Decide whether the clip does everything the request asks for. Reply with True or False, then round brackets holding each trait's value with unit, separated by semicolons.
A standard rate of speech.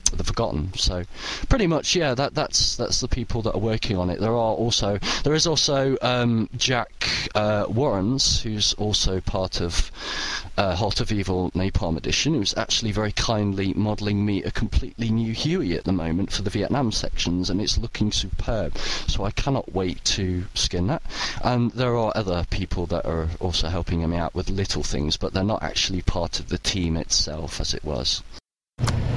True (185 wpm)